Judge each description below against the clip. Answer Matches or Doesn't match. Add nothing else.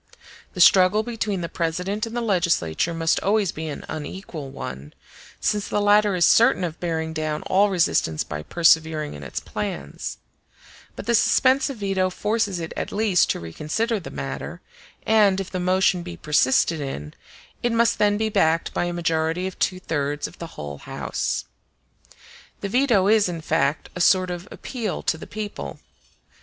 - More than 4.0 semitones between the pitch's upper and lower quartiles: Matches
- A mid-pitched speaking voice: Matches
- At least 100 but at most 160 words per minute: Doesn't match